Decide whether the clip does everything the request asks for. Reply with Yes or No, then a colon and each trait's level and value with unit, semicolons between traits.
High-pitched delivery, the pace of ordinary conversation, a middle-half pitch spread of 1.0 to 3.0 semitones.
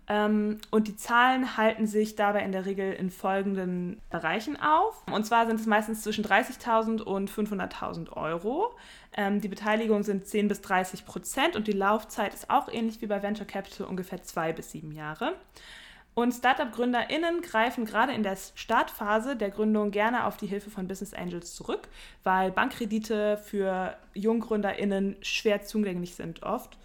Yes: high, 210 Hz; average, 160 wpm; narrow, 2.4 semitones